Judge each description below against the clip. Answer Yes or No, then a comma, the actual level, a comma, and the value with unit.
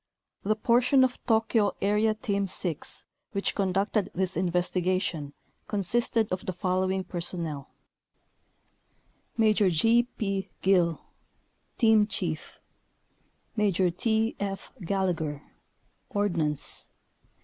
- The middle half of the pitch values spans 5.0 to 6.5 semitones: No, average, 3.4 semitones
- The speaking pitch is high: Yes, high, 195 Hz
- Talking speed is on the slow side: Yes, slow, 95 wpm